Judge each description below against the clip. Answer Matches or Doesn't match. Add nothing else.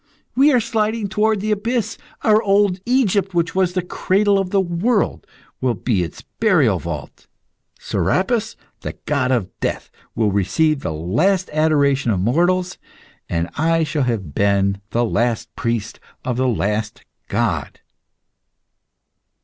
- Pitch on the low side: Doesn't match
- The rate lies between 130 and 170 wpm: Matches